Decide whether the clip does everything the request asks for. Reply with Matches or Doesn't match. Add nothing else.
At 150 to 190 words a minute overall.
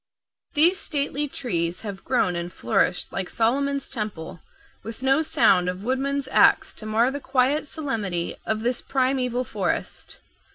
Doesn't match